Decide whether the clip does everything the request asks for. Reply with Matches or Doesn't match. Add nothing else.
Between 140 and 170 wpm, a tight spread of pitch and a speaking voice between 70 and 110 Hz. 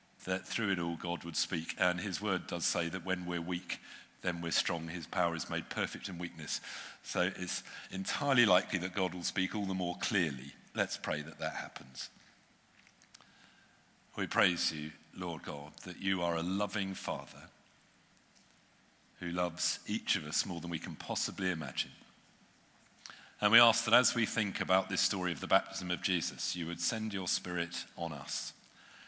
Doesn't match